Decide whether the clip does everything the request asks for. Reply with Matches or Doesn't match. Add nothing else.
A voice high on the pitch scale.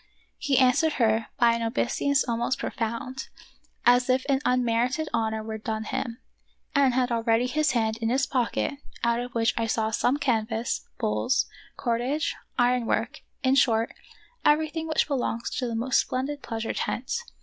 Matches